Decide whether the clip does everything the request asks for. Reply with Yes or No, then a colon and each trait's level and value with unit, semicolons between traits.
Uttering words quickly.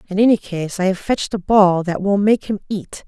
Yes: fast, 255 wpm